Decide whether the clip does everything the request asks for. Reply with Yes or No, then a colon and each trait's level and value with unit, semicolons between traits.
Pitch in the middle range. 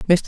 Yes: medium, 175 Hz